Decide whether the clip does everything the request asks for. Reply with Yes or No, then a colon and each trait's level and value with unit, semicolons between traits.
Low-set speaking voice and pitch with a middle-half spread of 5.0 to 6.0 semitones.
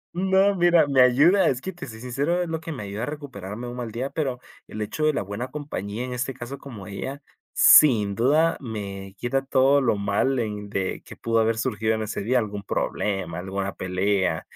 Yes: low, 120 Hz; wide, 5.5 semitones